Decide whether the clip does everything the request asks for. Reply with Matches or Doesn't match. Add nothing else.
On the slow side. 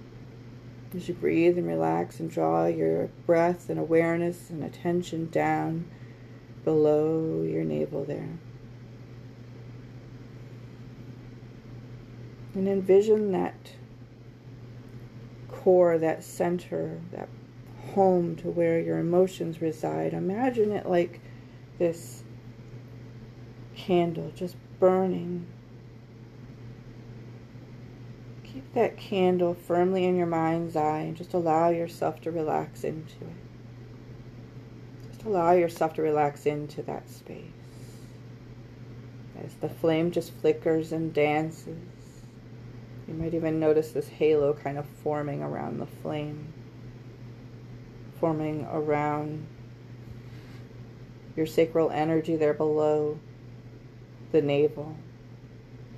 Matches